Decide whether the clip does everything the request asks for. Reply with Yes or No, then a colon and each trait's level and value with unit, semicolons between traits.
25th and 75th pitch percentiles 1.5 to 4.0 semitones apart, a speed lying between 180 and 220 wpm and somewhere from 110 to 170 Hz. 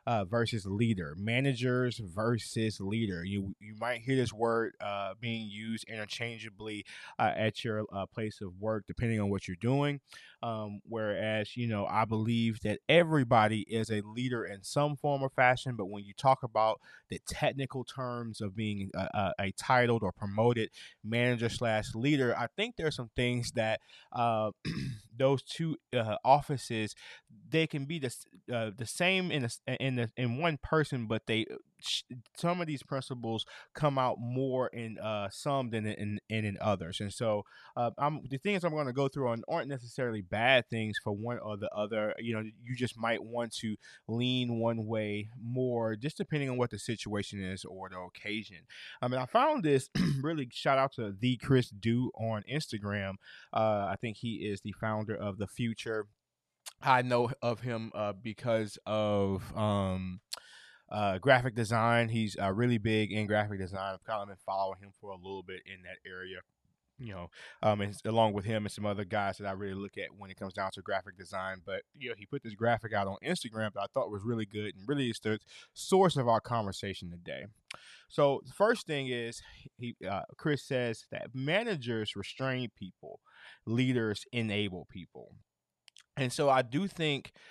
Yes: average, 3.5 semitones; average, 185 wpm; low, 115 Hz